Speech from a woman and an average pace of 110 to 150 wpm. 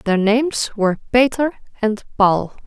Yes: female; slow, 135 wpm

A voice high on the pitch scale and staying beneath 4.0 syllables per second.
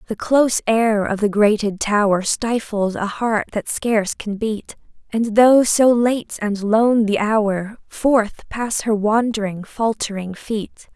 Yes: high, 215 Hz; 3.7 syllables/s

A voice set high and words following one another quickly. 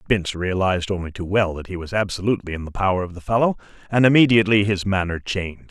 No: very low, 95 Hz; fast, 210 wpm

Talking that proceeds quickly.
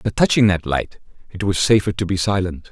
Yes: fast, 220 wpm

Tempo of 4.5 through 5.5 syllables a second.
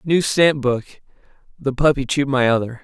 No: 2.8 syllables/s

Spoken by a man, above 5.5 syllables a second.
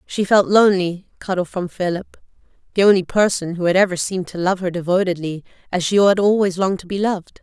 No: female; 6.1 syllables/s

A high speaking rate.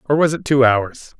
Yes: fast, 250 wpm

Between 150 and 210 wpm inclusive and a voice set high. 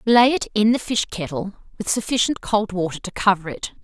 Yes: fast, 205 wpm; high, 210 Hz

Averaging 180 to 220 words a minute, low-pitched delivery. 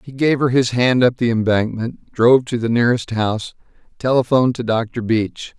Yes: average, 185 wpm; low, 120 Hz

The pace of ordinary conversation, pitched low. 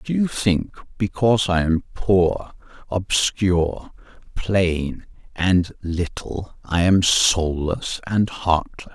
No: slow, 105 wpm; very low, 90 Hz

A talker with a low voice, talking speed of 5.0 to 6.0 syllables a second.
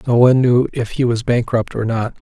Yes: low, 120 Hz; 5.5 syllables/s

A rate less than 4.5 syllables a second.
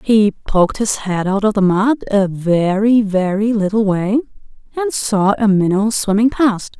Yes: 4.3 syllables/s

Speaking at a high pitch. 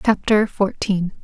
Yes: high, 200 Hz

